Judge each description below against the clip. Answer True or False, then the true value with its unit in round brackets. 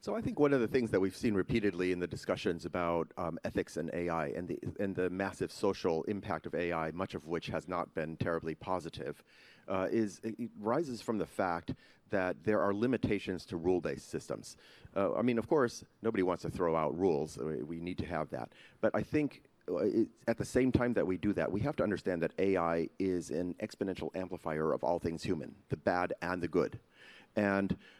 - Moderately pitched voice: False (95 Hz)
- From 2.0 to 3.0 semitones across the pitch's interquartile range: False (4.5 semitones)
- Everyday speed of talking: False (210 wpm)